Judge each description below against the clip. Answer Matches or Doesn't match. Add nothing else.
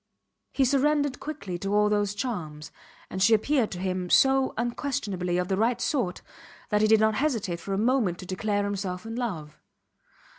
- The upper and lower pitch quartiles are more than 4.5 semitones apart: Matches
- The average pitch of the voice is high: Matches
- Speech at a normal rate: Matches